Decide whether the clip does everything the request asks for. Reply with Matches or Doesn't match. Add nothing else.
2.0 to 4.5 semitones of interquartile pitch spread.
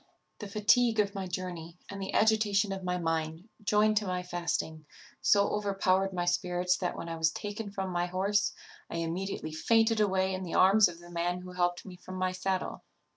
Matches